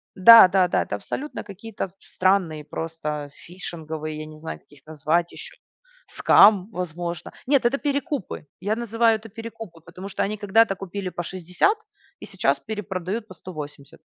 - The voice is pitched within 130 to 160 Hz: No, medium, 185 Hz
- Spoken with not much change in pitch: No, average, 5.1 semitones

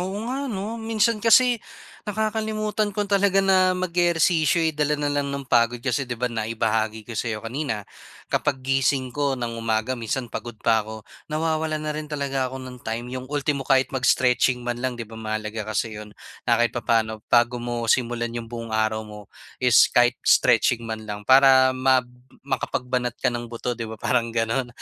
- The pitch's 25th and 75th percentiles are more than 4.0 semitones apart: Yes, average, 4.8 semitones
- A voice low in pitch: Yes, low, 125 Hz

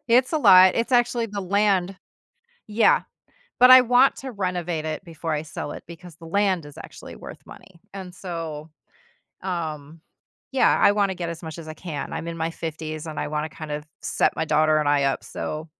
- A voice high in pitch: No, medium, 170 Hz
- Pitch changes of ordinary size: Yes, average, 4.2 semitones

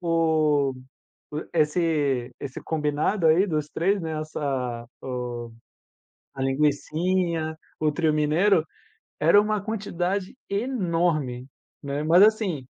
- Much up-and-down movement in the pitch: No, average, 3.9 semitones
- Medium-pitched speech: Yes, medium, 155 Hz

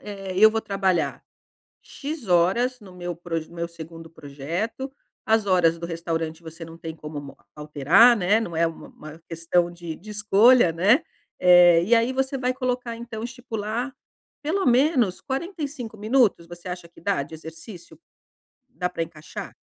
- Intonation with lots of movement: Yes, wide, 6.0 semitones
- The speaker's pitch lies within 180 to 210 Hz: Yes, medium, 185 Hz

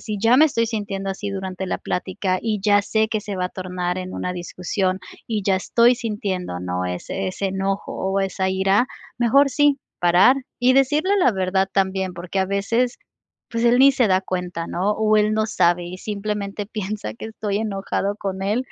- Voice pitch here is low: No, high, 195 Hz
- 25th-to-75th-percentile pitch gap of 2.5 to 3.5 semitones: Yes, average, 2.9 semitones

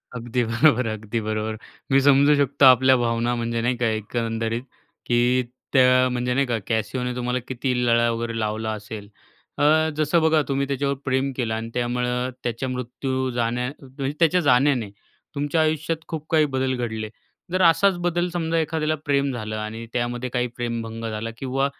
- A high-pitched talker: No, low, 125 Hz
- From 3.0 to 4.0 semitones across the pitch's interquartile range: Yes, average, 3.3 semitones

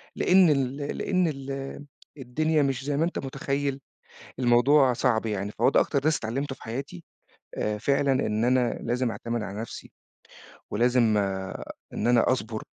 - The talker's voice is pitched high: No, low, 130 Hz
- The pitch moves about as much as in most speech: Yes, average, 3.2 semitones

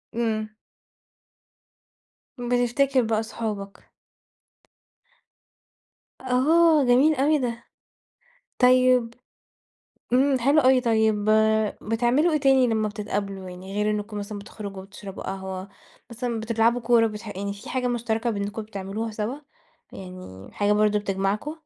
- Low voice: No, high, 225 Hz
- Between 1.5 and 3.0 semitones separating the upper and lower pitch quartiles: No, average, 3.5 semitones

